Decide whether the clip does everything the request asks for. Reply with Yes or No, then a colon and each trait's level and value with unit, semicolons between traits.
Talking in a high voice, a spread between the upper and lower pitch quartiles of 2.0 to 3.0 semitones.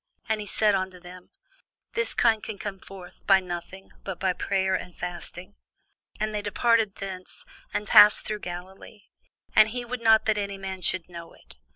Yes: high, 195 Hz; average, 2.7 semitones